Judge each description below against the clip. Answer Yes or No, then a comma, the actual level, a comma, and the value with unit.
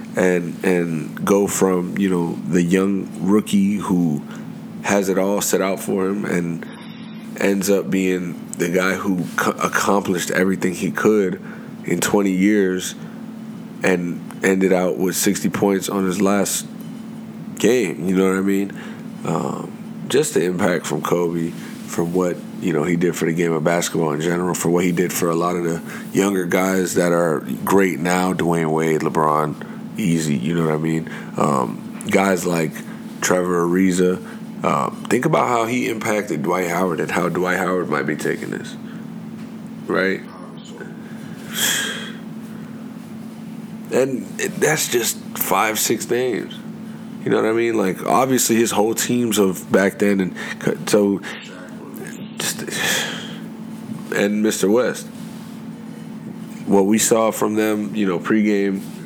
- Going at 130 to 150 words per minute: Yes, average, 145 wpm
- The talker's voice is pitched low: Yes, low, 100 Hz